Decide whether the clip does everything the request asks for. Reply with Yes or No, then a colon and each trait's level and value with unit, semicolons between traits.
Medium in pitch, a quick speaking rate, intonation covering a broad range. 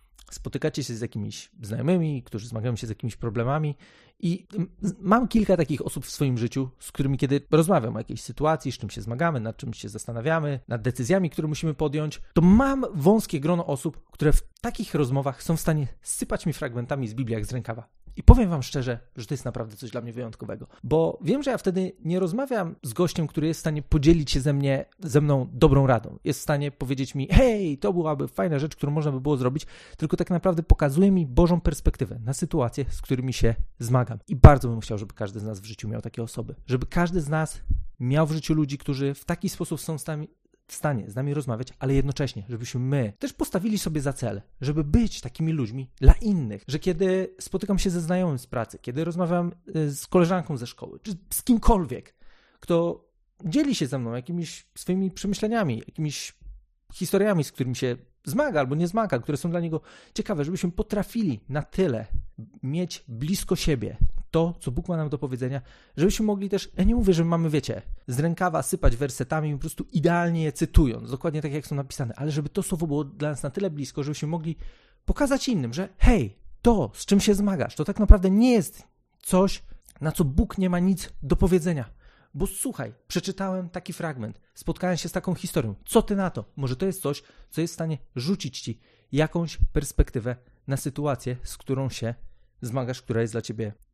Yes: medium, 150 Hz; fast, 200 wpm; wide, 5.9 semitones